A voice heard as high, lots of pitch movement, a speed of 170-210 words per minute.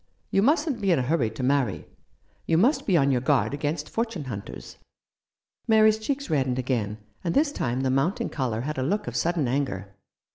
No: medium, 145 Hz; wide, 7.5 semitones; average, 190 wpm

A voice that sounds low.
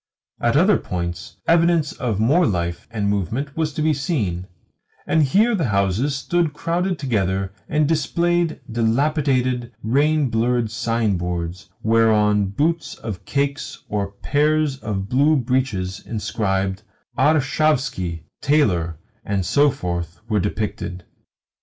Yes: low, 120 Hz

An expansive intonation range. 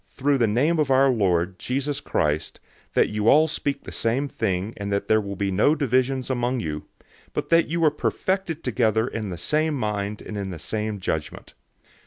Yes: wide, 5.8 semitones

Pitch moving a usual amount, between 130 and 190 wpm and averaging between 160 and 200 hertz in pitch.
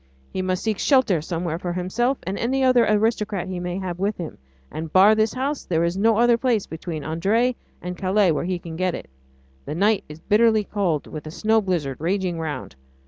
No: average, 4.4 semitones; fast, 205 wpm; medium, 185 Hz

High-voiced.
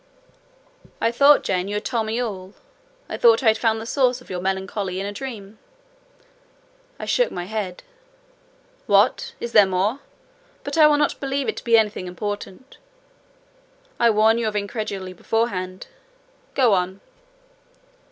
Yes: high, 215 Hz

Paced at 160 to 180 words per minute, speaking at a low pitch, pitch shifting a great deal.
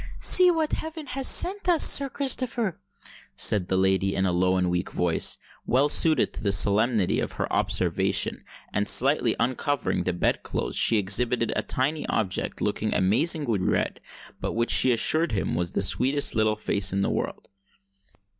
Yes: average, 170 wpm; low, 115 Hz; wide, 8.6 semitones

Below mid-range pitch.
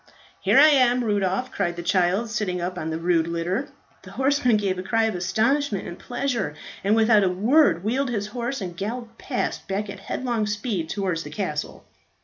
No: high, 205 Hz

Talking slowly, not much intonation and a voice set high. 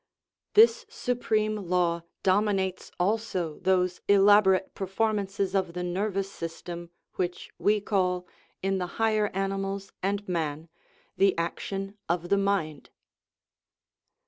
Yes: slow, 115 wpm; narrow, 2.3 semitones; high, 195 Hz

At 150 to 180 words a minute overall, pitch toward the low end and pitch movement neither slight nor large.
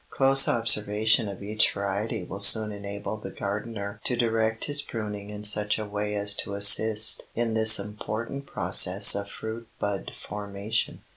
No: average, 155 wpm; low, 105 Hz; narrow, 1.7 semitones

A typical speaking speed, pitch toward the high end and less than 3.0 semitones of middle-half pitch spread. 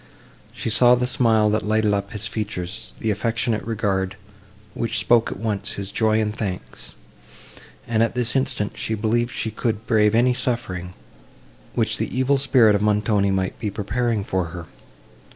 No: average, 160 wpm; low, 110 Hz; narrow, 2.5 semitones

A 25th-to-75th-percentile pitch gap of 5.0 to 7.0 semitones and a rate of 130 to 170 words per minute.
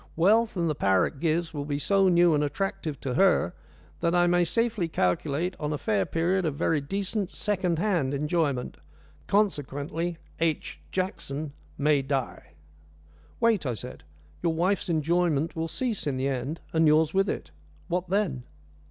No: average, 4.3 semitones; average, 160 wpm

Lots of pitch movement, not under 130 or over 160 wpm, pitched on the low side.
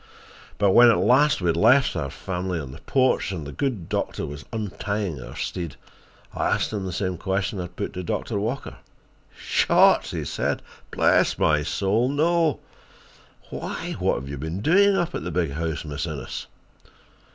No: wide, 6.8 semitones; average, 180 wpm; very low, 95 Hz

